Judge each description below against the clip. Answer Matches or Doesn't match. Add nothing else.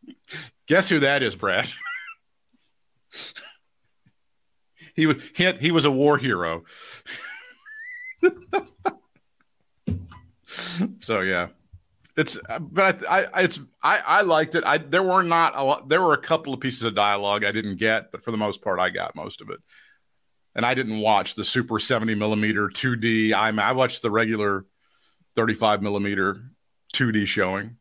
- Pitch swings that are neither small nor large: Doesn't match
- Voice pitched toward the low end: Matches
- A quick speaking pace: Doesn't match